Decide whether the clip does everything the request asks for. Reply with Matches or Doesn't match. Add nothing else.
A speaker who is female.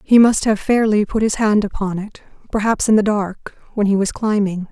Matches